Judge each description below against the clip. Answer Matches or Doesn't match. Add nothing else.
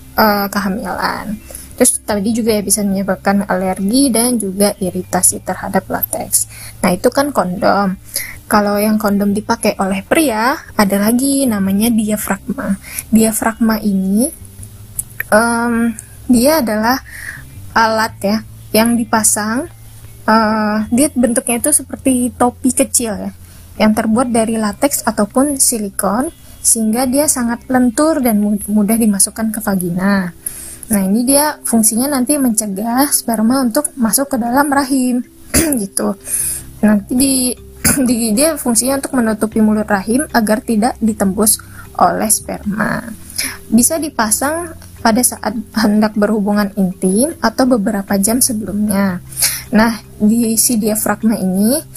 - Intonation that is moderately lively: Matches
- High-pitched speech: Matches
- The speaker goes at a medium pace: Matches